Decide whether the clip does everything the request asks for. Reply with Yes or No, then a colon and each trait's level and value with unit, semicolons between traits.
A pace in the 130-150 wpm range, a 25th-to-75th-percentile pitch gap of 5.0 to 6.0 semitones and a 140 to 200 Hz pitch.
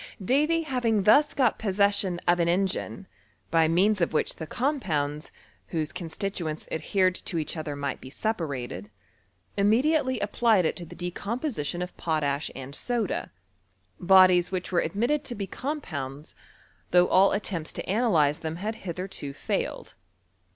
Yes: average, 145 wpm; wide, 5.6 semitones; medium, 185 Hz